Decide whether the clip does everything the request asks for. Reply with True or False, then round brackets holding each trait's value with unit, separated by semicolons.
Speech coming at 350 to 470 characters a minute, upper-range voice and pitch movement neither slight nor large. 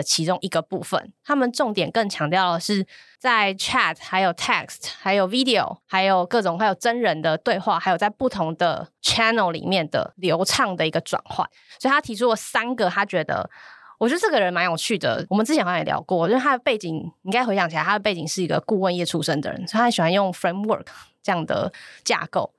True (380 characters per minute; 195 Hz; 4.7 semitones)